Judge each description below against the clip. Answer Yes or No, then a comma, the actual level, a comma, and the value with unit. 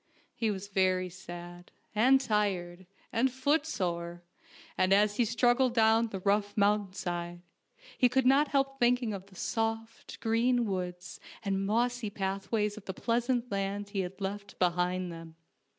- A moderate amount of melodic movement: Yes, average, 4.1 semitones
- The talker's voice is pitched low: No, high, 205 Hz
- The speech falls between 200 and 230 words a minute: No, average, 150 wpm